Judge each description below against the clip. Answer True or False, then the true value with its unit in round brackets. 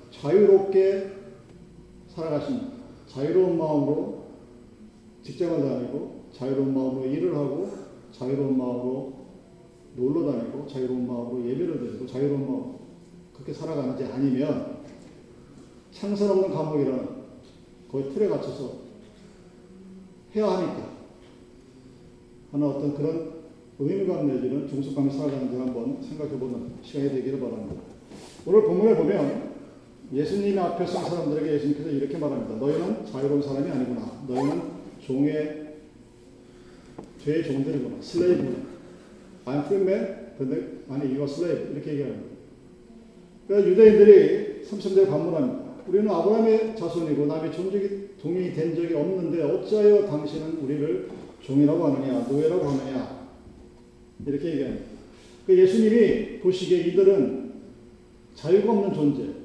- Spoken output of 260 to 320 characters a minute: False (340 characters per minute)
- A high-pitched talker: False (150 Hz)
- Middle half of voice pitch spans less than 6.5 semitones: True (6.1 semitones)